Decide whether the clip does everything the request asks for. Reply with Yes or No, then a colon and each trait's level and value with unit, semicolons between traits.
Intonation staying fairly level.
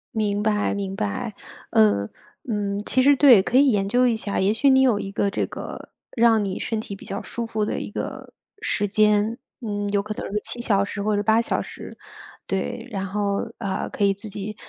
Yes: narrow, 2.2 semitones